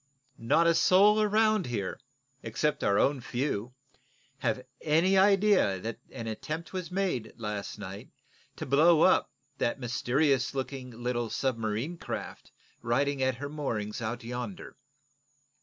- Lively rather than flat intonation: Yes, wide, 6.2 semitones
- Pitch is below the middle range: Yes, low, 130 Hz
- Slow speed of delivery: Yes, slow, 130 wpm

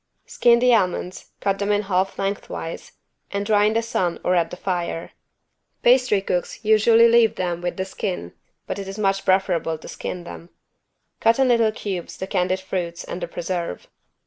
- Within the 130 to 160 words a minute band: No, average, 180 wpm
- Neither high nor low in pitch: No, high, 195 Hz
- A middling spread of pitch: Yes, average, 3.3 semitones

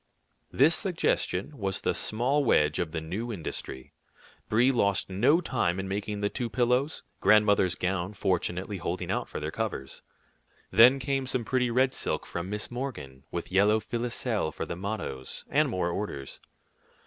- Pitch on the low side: Yes, low, 105 Hz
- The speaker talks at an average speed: Yes, average, 160 wpm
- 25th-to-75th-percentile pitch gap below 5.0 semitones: No, wide, 5.5 semitones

